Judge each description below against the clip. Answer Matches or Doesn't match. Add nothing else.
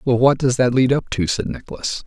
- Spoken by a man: Matches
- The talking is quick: Matches